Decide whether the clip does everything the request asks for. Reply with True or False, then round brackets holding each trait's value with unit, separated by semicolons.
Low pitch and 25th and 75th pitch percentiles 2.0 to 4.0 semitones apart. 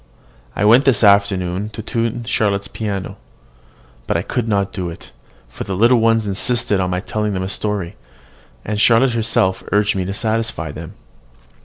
True (105 Hz; 3.1 semitones)